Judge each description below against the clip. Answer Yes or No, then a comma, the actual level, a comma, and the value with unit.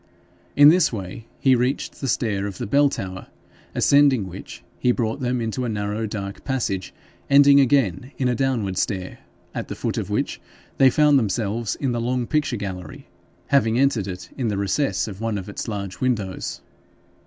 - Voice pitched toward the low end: Yes, low, 115 Hz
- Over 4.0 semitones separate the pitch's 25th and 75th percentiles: Yes, average, 5.1 semitones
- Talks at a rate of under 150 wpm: No, average, 180 wpm